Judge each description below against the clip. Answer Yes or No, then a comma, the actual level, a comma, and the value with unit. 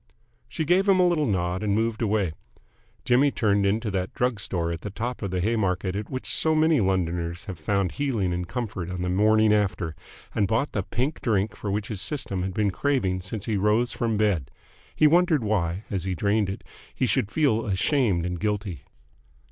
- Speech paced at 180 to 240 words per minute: Yes, average, 200 wpm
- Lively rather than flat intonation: No, average, 4.3 semitones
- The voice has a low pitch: Yes, low, 105 Hz